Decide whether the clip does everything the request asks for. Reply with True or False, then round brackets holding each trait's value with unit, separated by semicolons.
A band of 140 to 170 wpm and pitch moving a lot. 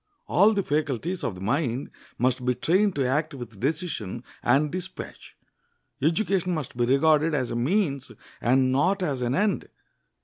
True (160 wpm; 5.8 semitones)